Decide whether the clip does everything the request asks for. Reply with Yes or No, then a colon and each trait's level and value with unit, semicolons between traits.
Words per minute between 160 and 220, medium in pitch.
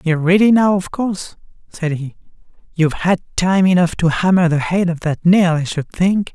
Yes: average, 200 wpm; medium, 175 Hz